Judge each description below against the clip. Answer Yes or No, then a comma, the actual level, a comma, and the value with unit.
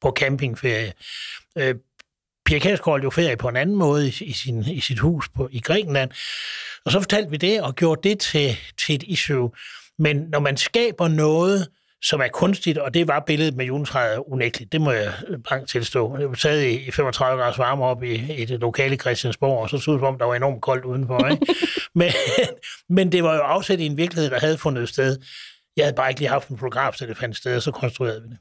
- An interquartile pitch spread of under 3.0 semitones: No, average, 4.2 semitones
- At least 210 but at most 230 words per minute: Yes, average, 220 wpm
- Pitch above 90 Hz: Yes, medium, 140 Hz